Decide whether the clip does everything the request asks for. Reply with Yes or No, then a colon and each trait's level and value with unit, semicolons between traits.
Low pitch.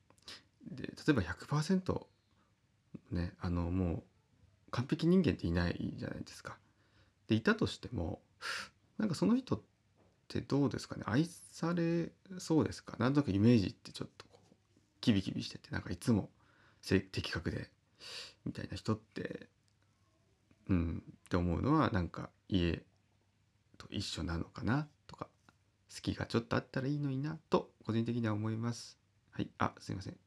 Yes: low, 105 Hz